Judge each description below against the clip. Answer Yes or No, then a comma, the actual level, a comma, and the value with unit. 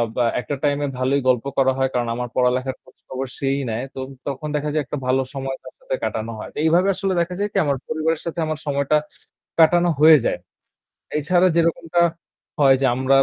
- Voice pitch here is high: No, medium, 140 Hz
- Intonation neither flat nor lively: Yes, average, 3.6 semitones